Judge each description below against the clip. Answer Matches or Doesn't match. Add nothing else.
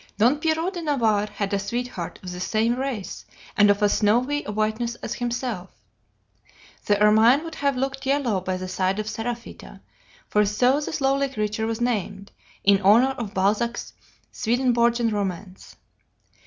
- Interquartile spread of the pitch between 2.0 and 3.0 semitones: Doesn't match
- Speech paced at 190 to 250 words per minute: Doesn't match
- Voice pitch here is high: Matches